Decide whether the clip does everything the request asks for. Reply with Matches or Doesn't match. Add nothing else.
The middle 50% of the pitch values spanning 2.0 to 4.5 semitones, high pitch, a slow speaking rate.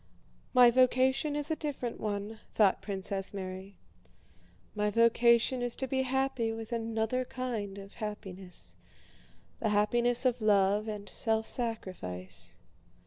Matches